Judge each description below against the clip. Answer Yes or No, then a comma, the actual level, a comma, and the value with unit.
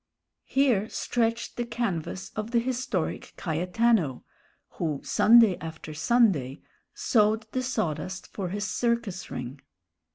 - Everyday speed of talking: No, slow, 110 wpm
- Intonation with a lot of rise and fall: Yes, wide, 6.2 semitones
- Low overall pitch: No, high, 210 Hz